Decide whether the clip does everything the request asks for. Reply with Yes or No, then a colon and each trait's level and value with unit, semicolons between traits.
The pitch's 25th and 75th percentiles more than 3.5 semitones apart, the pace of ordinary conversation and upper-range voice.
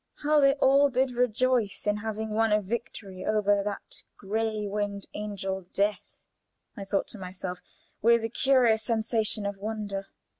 No: average, 2.7 semitones; average, 150 wpm; high, 215 Hz